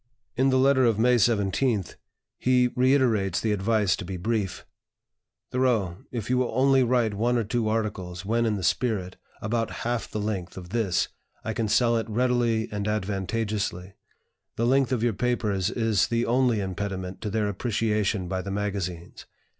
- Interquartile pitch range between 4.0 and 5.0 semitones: No, average, 3.5 semitones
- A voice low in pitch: Yes, low, 110 Hz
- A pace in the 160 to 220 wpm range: Yes, average, 170 wpm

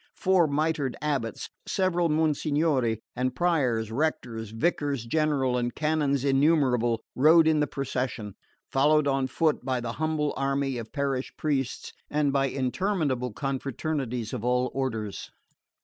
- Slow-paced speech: Yes, slow, 130 wpm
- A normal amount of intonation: Yes, average, 3.5 semitones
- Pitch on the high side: No, low, 135 Hz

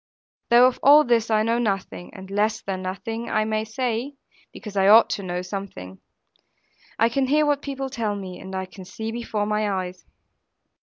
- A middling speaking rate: Yes, average, 190 wpm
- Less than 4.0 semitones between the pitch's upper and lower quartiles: Yes, average, 3.6 semitones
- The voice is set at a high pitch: Yes, high, 215 Hz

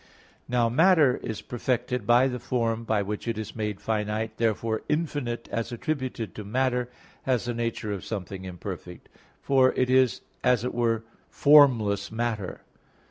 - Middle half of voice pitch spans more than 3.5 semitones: No, average, 2.8 semitones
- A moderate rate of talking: Yes, average, 150 wpm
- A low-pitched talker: Yes, low, 115 Hz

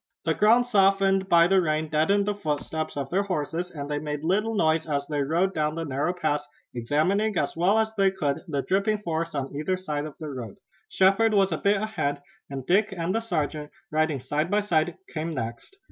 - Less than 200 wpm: No, fast, 205 wpm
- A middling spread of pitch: Yes, average, 4.8 semitones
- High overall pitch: No, medium, 165 Hz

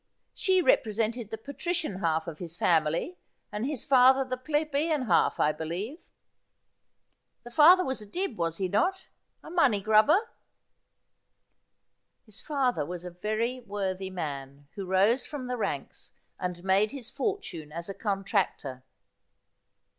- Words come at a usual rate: Yes, average, 145 wpm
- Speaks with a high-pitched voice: Yes, high, 215 Hz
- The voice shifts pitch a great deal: Yes, wide, 7.3 semitones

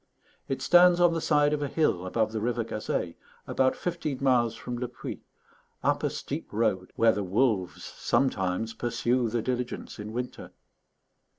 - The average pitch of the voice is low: Yes, low, 120 Hz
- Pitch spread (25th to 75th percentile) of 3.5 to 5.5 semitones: Yes, average, 3.8 semitones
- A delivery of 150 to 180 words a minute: Yes, average, 165 wpm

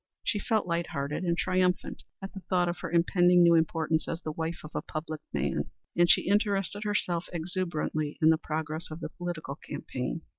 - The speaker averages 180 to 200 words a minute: Yes, average, 190 wpm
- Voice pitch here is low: No, medium, 170 Hz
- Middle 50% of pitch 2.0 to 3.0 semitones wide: Yes, narrow, 2.4 semitones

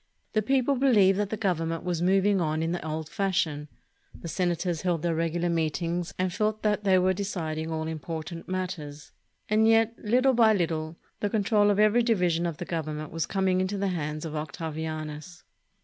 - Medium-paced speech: Yes, average, 190 wpm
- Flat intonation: No, average, 4.2 semitones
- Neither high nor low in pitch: Yes, medium, 175 Hz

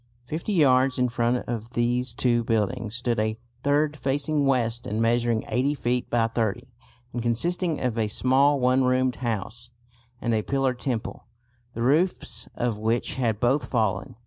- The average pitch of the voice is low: Yes, low, 120 Hz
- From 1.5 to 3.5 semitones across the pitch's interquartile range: Yes, narrow, 2.5 semitones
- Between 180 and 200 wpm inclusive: No, average, 160 wpm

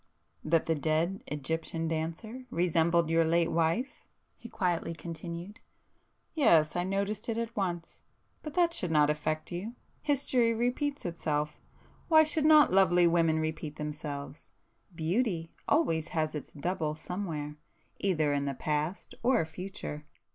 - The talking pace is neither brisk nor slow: No, slow, 130 wpm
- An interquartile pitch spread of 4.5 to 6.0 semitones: Yes, average, 5.0 semitones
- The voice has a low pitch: No, medium, 170 Hz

